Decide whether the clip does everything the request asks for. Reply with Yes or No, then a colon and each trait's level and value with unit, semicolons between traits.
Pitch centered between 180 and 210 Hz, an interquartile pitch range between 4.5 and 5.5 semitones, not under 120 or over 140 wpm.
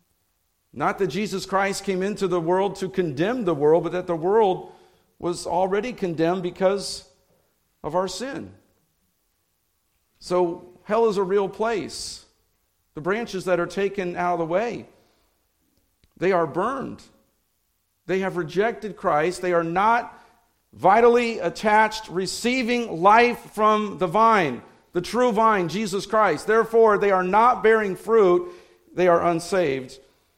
No: high, 190 Hz; average, 3.7 semitones; slow, 135 wpm